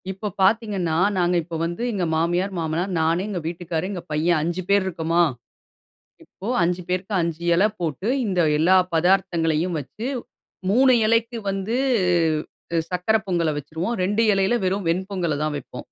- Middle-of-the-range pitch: Yes, medium, 180 Hz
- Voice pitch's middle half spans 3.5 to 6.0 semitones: No, average, 2.9 semitones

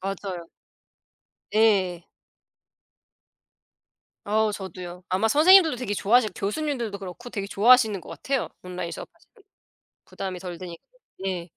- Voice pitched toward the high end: Yes, high, 200 Hz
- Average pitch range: Yes, average, 4.4 semitones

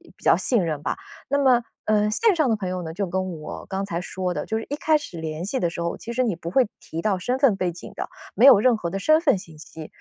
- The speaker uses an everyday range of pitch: No, wide, 6.5 semitones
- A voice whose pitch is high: Yes, high, 200 Hz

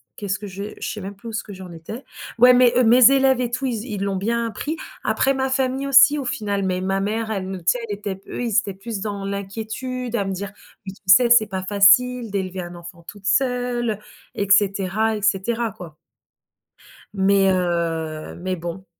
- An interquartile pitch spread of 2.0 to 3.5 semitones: No, average, 3.9 semitones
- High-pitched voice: Yes, high, 205 Hz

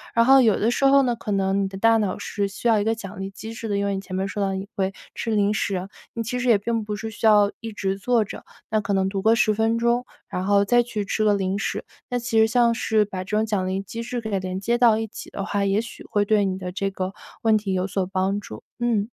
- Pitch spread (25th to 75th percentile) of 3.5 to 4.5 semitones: No, narrow, 2.6 semitones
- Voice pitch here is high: Yes, high, 210 Hz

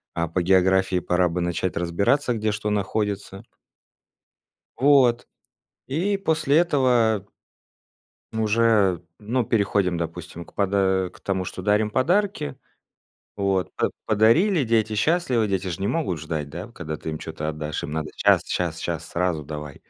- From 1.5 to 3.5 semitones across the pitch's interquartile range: No, average, 4.9 semitones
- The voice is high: No, low, 100 Hz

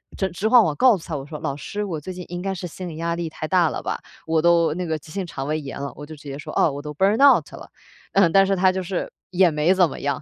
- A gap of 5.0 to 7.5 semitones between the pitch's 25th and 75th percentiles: No, average, 3.8 semitones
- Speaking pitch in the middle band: Yes, medium, 170 Hz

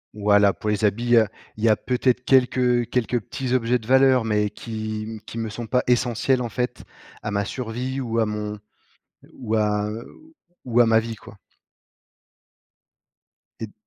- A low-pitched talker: Yes, low, 115 Hz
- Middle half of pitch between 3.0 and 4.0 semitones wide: No, narrow, 2.6 semitones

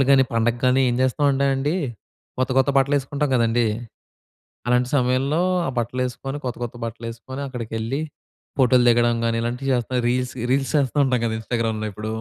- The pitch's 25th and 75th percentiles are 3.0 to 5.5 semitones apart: No, narrow, 2.5 semitones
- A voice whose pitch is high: No, low, 125 Hz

